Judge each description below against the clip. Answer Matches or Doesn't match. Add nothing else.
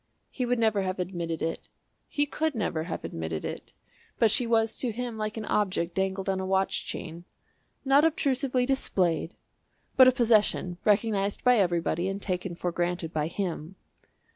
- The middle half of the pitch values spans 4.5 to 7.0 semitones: Matches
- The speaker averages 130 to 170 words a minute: Matches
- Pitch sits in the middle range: Doesn't match